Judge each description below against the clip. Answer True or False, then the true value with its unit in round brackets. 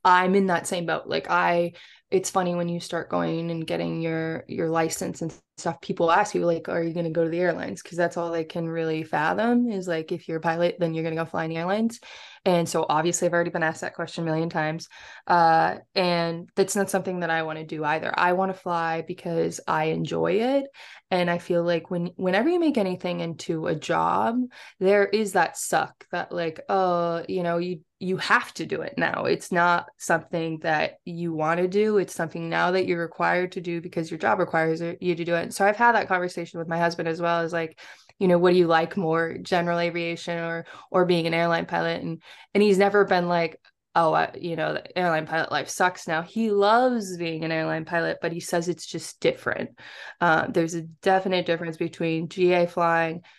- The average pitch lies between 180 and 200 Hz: False (170 Hz)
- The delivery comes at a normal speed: False (225 wpm)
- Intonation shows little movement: True (1.8 semitones)